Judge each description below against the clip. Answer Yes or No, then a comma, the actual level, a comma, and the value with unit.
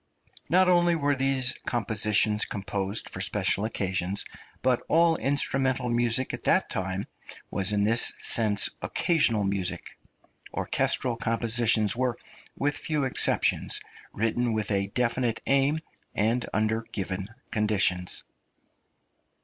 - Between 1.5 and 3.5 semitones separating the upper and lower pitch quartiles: No, average, 4.3 semitones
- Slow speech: Yes, slow, 115 wpm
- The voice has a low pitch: Yes, low, 115 Hz